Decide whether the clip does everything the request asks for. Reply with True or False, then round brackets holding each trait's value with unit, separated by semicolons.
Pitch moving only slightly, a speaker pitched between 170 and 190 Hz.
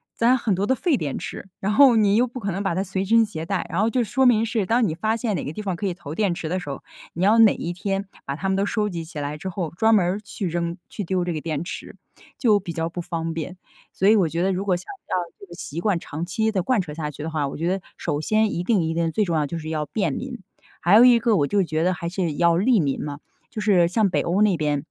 False (4.4 semitones; 185 Hz)